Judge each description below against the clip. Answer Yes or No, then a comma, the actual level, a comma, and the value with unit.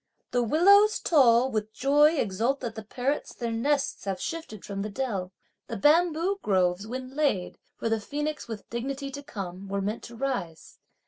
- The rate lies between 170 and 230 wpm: Yes, average, 175 wpm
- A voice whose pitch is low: No, high, 240 Hz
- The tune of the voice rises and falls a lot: Yes, wide, 5.8 semitones